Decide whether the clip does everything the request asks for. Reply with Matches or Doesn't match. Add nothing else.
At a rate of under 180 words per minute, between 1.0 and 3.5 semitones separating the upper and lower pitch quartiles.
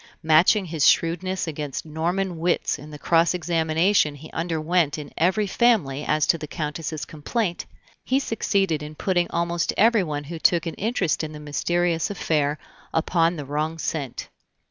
Matches